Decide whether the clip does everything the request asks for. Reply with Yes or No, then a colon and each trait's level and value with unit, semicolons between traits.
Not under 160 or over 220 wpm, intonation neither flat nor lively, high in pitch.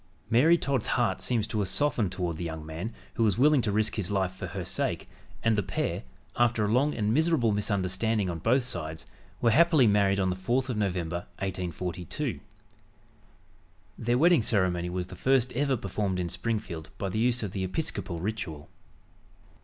No: average, 180 wpm; average, 4.8 semitones; low, 105 Hz